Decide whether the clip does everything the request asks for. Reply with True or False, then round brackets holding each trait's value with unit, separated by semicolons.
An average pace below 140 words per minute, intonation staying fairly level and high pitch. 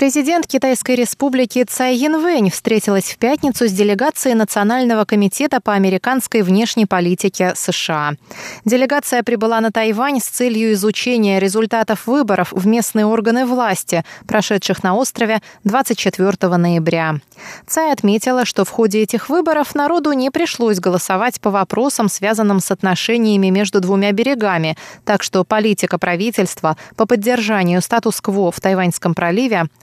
False (130 wpm; 4.4 semitones; 220 Hz)